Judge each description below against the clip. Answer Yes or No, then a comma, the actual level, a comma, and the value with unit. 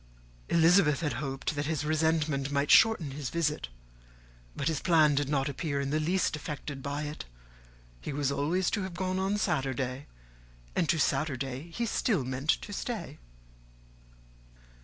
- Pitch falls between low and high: Yes, medium, 150 Hz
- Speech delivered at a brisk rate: No, average, 155 wpm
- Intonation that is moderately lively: Yes, average, 3.3 semitones